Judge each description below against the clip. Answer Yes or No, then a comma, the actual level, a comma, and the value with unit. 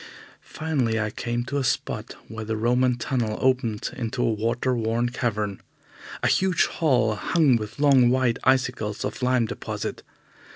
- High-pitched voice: No, low, 120 Hz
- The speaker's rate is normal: Yes, average, 155 wpm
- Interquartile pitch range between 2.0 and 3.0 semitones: Yes, narrow, 2.6 semitones